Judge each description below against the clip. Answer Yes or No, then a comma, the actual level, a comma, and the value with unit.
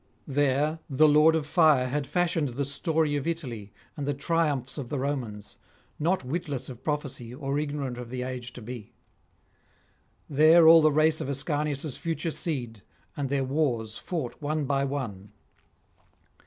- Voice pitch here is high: No, medium, 145 Hz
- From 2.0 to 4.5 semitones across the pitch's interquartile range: Yes, average, 3.3 semitones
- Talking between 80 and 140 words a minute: No, average, 155 wpm